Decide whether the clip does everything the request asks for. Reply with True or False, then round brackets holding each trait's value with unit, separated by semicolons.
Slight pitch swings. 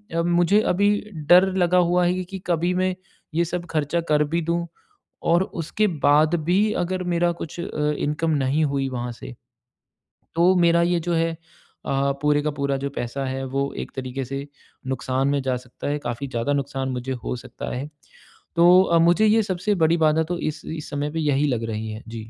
False (4.3 semitones)